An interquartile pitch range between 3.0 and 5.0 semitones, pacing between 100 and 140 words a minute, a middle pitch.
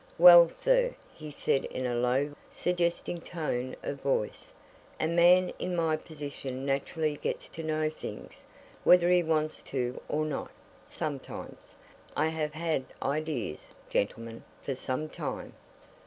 Yes: average, 3.8 semitones; slow, 135 wpm; medium, 155 Hz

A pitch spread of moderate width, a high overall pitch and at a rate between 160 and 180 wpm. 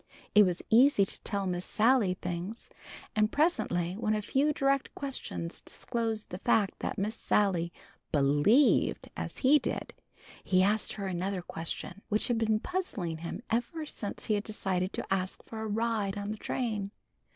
Yes: average, 3.9 semitones; high, 210 Hz; average, 165 wpm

